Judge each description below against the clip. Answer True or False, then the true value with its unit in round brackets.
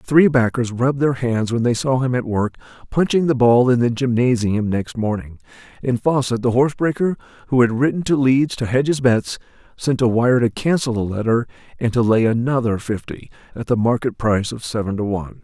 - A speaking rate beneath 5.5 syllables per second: False (5.6 syllables/s)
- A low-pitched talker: True (120 Hz)